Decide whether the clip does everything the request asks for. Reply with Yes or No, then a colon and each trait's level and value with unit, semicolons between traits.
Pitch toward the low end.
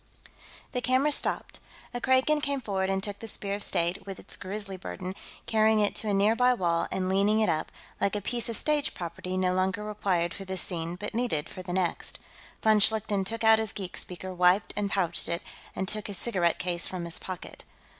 No: high, 195 Hz